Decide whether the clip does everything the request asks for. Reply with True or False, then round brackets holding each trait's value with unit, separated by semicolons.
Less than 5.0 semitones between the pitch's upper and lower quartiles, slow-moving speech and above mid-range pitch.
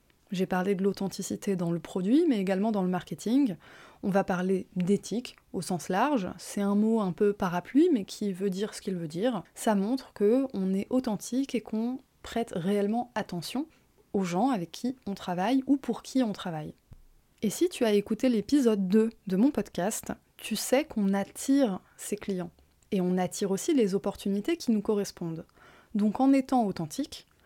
False (4.4 semitones; 180 wpm; 205 Hz)